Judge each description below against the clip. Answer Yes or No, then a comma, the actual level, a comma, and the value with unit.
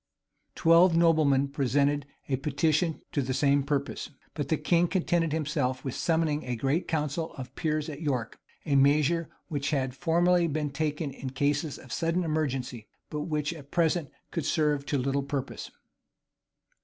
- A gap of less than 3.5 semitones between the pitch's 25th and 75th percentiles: Yes, average, 2.7 semitones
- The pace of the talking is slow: No, average, 165 wpm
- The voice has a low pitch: No, medium, 150 Hz